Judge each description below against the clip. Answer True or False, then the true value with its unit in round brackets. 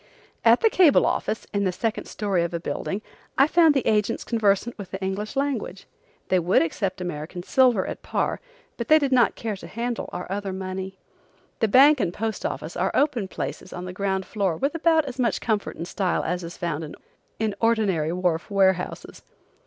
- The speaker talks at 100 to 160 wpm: False (190 wpm)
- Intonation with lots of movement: False (4.5 semitones)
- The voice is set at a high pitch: True (200 Hz)